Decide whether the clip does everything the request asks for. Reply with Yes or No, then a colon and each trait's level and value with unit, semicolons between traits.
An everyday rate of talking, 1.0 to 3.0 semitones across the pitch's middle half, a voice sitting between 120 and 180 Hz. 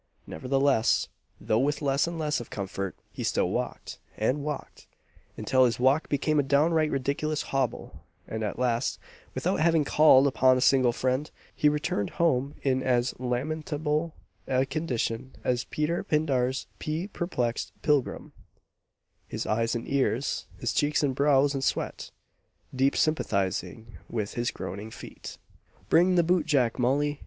No: average, 145 wpm; average, 3.6 semitones; low, 135 Hz